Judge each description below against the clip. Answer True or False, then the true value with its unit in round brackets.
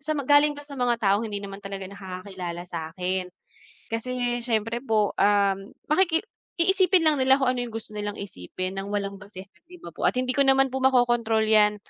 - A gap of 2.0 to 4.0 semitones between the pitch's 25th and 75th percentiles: False (5.0 semitones)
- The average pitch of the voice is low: False (220 Hz)